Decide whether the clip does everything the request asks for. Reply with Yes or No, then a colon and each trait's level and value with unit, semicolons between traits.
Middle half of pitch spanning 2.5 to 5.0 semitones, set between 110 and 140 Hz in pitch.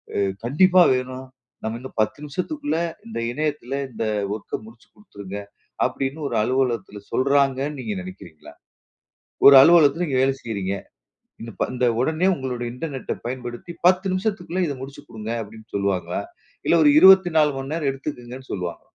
No: wide, 5.4 semitones; low, 135 Hz